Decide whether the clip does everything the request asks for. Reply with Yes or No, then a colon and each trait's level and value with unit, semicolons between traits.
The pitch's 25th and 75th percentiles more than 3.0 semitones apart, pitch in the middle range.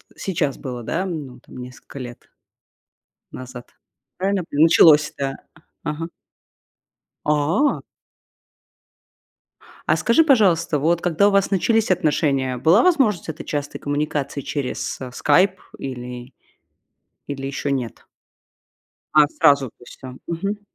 Yes: average, 5.3 semitones; medium, 150 Hz